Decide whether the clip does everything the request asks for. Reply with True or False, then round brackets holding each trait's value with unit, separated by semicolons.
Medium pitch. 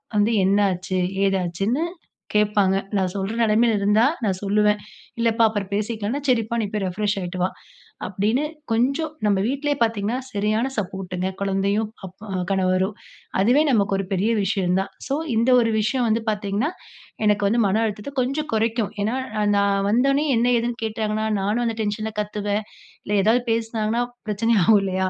False (210 Hz)